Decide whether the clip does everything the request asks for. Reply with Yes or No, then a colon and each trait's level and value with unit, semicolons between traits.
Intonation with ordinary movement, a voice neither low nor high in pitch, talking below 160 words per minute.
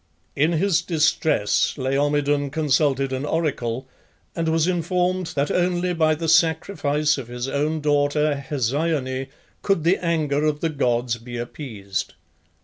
Yes: average, 3.4 semitones; medium, 150 Hz; slow, 135 wpm